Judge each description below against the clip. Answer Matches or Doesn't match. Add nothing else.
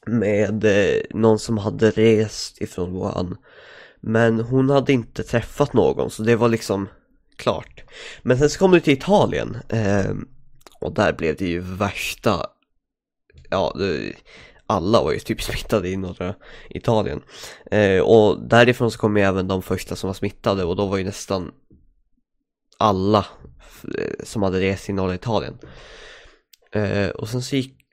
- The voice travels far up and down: Doesn't match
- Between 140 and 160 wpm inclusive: Matches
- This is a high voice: Doesn't match